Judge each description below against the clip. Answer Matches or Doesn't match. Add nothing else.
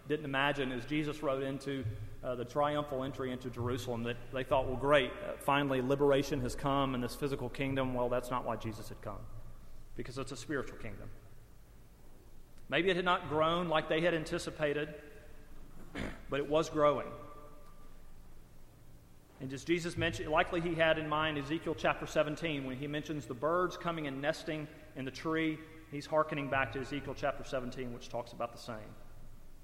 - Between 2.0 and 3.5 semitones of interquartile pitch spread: Doesn't match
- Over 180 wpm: Doesn't match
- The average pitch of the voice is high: Doesn't match